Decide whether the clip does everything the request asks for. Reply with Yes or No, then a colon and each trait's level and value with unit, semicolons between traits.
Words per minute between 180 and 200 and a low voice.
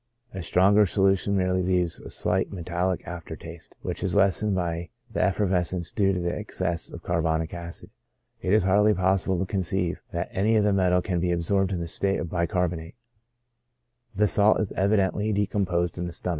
Yes: average, 190 wpm; very low, 90 Hz